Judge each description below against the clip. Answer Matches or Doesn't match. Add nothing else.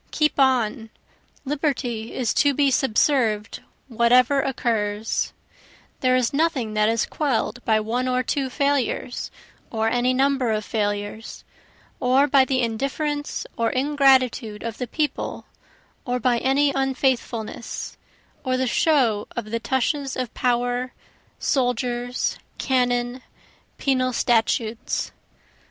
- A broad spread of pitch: Doesn't match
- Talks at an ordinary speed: Doesn't match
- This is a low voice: Doesn't match